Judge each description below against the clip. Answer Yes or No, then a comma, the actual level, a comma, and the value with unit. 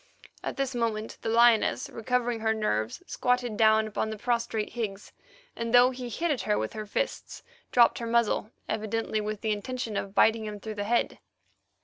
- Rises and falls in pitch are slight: Yes, narrow, 2.1 semitones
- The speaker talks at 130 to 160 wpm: No, average, 185 wpm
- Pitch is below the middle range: No, high, 225 Hz